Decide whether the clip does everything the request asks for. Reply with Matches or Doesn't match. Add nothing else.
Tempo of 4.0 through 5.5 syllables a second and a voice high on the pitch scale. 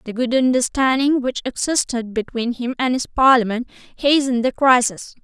Matches